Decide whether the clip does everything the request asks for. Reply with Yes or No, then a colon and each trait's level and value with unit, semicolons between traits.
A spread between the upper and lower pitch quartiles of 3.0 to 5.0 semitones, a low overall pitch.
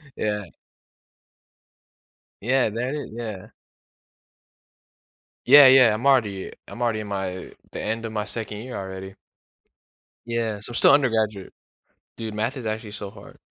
No: narrow, 2.6 semitones; low, 110 Hz